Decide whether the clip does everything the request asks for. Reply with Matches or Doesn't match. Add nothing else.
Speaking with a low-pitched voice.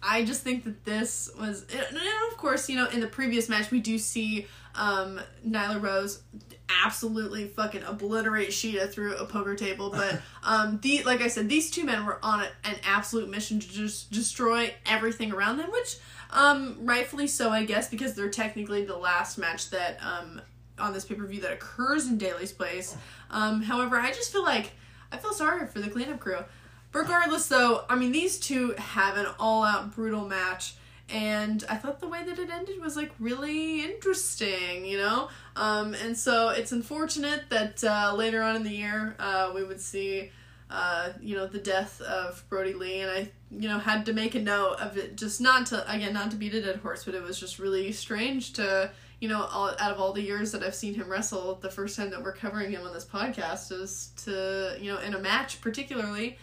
Doesn't match